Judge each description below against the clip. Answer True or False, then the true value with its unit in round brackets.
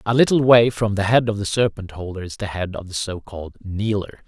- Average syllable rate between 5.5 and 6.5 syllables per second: True (5.8 syllables/s)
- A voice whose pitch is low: True (105 Hz)